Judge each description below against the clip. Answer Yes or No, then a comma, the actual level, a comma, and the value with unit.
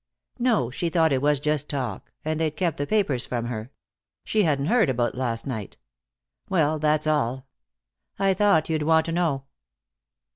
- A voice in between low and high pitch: Yes, medium, 150 Hz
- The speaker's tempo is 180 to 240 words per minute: No, average, 170 wpm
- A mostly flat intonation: No, average, 4.1 semitones